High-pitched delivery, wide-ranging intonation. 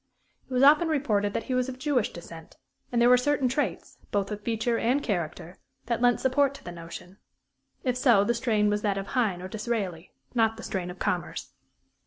No: high, 225 Hz; average, 4.4 semitones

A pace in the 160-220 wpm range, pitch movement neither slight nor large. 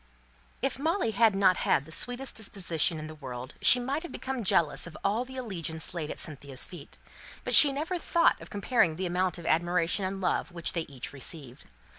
No: average, 200 wpm; wide, 7.4 semitones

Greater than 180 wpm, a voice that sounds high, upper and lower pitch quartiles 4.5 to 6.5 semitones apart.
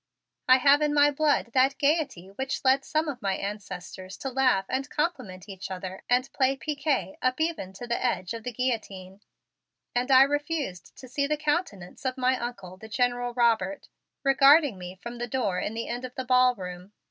Yes: average, 190 wpm; very high, 250 Hz; wide, 5.6 semitones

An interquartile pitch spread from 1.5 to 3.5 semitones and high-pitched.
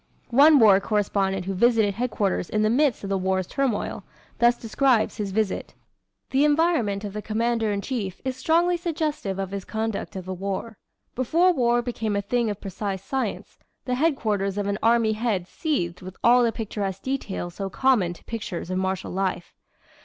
No: average, 4.3 semitones; high, 215 Hz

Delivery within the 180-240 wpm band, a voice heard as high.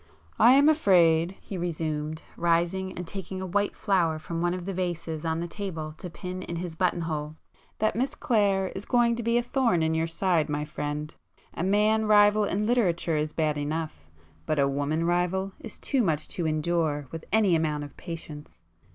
No: average, 185 wpm; medium, 170 Hz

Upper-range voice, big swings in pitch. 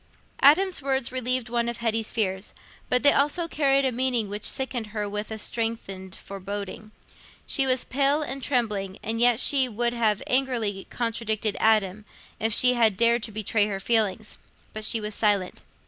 No: high, 230 Hz; average, 3.3 semitones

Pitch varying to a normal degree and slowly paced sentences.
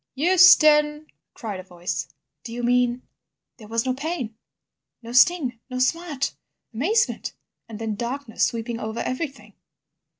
Yes: average, 4.7 semitones; slow, 130 wpm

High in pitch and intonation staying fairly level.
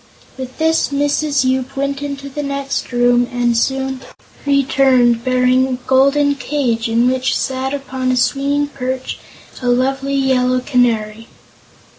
Yes: very high, 260 Hz; narrow, 1.8 semitones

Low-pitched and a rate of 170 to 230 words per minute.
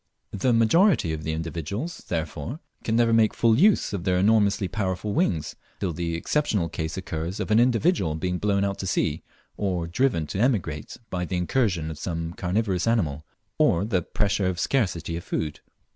Yes: very low, 95 Hz; average, 175 wpm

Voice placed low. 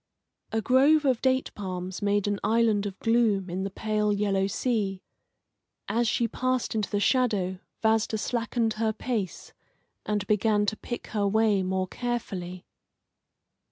No: high, 215 Hz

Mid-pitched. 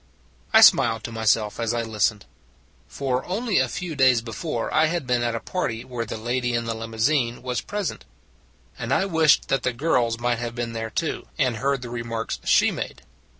No: low, 120 Hz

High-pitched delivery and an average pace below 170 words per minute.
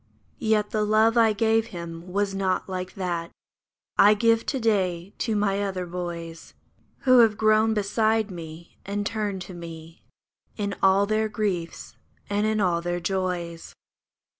Yes: high, 200 Hz; average, 150 wpm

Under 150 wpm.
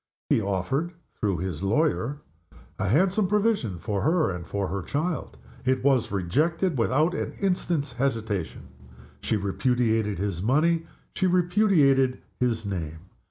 Yes: slow, 135 wpm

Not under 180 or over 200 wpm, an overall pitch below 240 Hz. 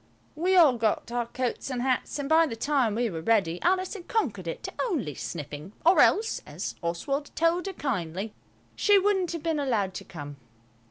No: average, 195 wpm; very high, 255 Hz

